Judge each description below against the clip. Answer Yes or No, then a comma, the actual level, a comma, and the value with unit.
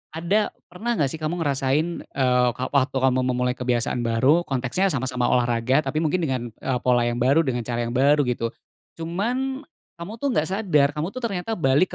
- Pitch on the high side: No, medium, 140 Hz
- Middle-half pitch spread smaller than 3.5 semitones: No, average, 5.3 semitones